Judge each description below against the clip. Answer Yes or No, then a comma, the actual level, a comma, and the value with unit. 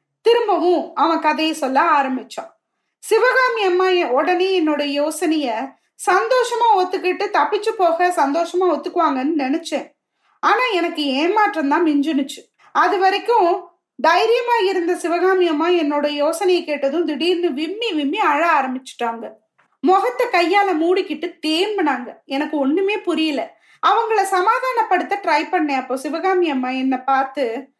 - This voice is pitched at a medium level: No, very high, 345 Hz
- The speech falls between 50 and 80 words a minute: No, average, 110 wpm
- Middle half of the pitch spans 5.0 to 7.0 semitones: No, average, 4.4 semitones